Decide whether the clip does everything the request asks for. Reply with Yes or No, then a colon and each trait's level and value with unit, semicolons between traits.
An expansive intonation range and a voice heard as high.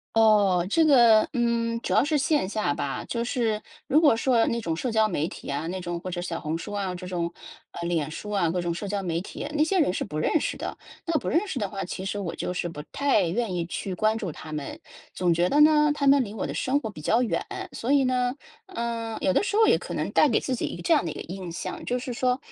Yes: wide, 6.2 semitones; high, 215 Hz